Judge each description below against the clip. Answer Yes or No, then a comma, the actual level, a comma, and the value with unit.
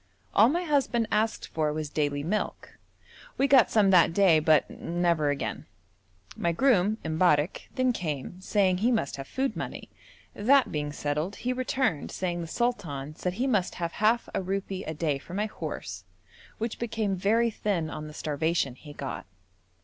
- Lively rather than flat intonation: Yes, wide, 6.5 semitones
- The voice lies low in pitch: No, medium, 185 Hz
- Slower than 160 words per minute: No, average, 170 wpm